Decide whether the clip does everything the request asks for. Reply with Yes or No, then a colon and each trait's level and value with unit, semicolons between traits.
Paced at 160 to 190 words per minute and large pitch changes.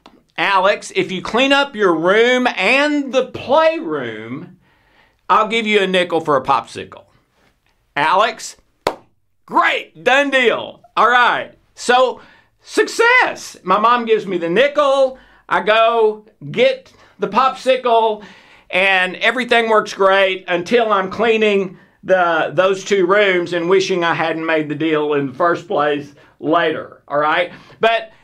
No: slow, 135 wpm; wide, 5.7 semitones